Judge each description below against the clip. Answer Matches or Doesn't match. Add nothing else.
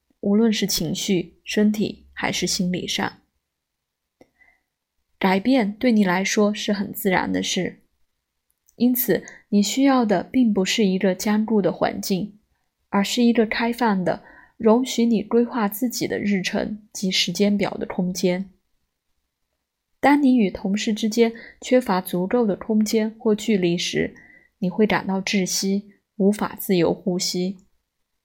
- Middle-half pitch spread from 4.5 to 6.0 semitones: Doesn't match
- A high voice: Matches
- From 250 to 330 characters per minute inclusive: Doesn't match